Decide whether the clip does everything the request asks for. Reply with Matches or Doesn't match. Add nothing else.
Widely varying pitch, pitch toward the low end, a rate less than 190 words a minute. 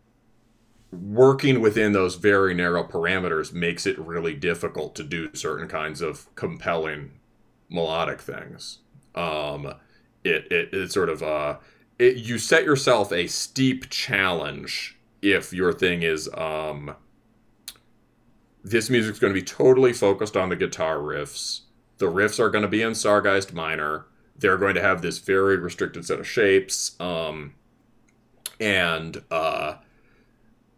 Matches